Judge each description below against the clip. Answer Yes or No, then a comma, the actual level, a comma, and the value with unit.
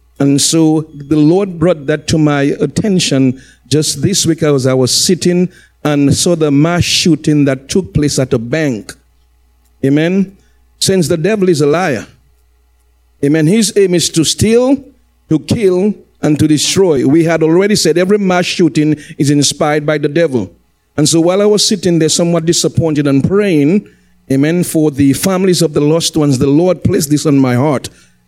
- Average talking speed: Yes, average, 175 wpm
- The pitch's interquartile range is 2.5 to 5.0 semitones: Yes, average, 4.1 semitones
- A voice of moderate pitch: Yes, medium, 155 Hz